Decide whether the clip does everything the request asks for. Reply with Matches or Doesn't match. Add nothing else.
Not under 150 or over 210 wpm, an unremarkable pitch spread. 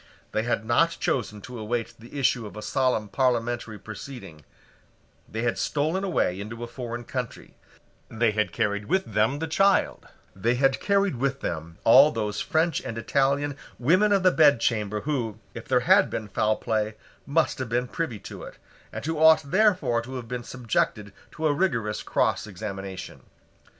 Matches